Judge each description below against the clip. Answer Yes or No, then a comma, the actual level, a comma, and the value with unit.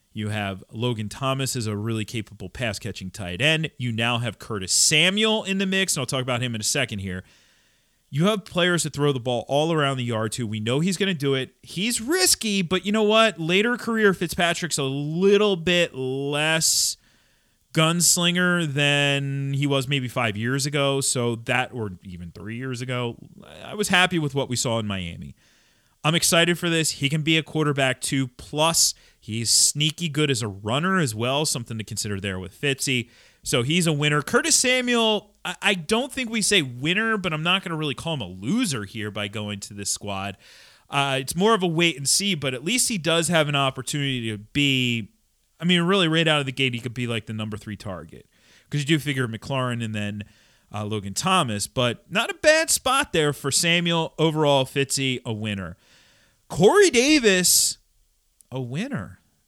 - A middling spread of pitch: No, wide, 7.0 semitones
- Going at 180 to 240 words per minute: Yes, average, 200 wpm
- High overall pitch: No, medium, 140 Hz